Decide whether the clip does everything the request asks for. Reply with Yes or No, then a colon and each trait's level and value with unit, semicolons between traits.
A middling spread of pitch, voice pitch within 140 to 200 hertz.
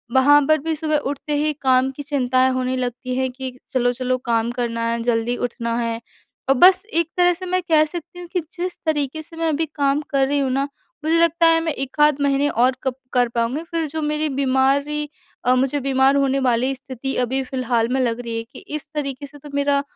No: average, 3.1 semitones; very high, 275 Hz